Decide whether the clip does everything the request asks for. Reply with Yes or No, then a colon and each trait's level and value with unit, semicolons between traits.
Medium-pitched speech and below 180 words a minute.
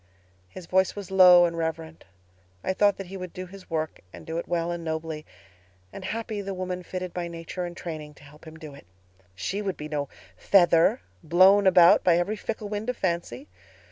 No: medium, 175 Hz; fast, 205 wpm